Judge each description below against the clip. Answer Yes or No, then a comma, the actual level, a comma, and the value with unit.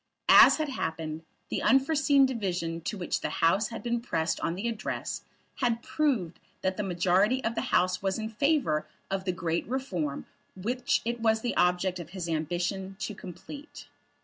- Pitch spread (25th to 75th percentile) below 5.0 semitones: No, wide, 5.4 semitones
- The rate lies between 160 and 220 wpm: Yes, average, 175 wpm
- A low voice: No, high, 195 Hz